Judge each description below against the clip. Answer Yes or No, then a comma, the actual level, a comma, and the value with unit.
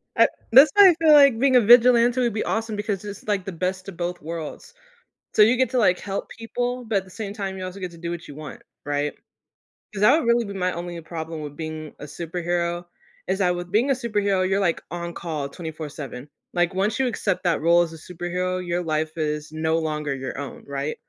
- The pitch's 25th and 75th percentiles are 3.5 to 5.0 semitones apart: Yes, average, 4.7 semitones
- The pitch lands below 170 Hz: No, medium, 180 Hz